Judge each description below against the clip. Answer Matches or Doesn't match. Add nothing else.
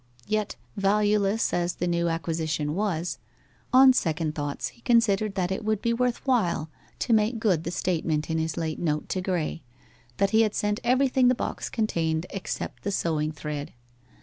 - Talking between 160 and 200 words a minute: Matches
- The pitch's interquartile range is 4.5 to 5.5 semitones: Matches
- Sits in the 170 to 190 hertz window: Matches